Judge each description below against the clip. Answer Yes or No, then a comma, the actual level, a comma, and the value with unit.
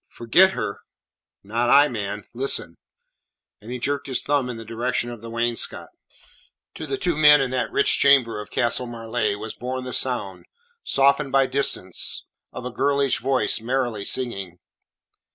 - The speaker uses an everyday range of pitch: Yes, average, 3.2 semitones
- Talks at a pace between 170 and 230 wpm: No, average, 160 wpm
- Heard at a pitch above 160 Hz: No, low, 125 Hz